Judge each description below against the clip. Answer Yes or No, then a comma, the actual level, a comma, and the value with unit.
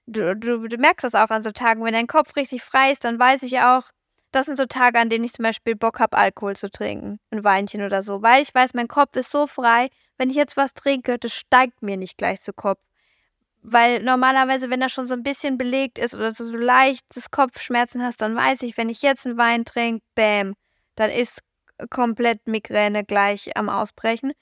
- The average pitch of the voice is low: No, high, 240 Hz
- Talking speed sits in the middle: No, fast, 220 wpm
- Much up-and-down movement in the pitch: No, narrow, 2.6 semitones